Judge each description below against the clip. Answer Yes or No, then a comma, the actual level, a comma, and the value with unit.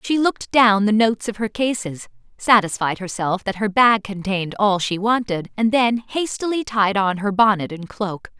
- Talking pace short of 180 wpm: No, average, 185 wpm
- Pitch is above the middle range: Yes, high, 210 Hz